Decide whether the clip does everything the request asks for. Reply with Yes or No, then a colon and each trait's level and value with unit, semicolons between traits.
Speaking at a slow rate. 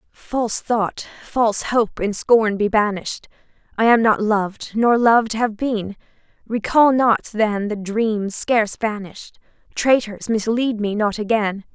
Yes: slow, 130 wpm